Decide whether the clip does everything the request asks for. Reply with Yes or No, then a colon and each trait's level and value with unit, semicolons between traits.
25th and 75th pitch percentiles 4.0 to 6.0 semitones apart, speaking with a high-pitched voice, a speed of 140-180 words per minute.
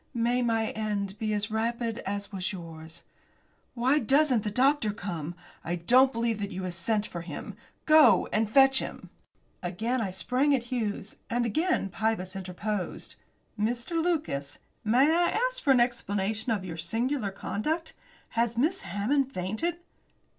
Yes: average, 4.9 semitones; high, 220 Hz; average, 155 wpm